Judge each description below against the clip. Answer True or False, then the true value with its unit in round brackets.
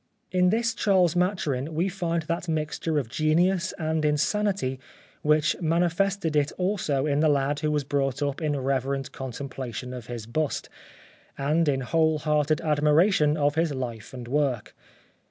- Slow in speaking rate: False (155 wpm)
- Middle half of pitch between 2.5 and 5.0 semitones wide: True (3.6 semitones)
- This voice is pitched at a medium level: True (150 Hz)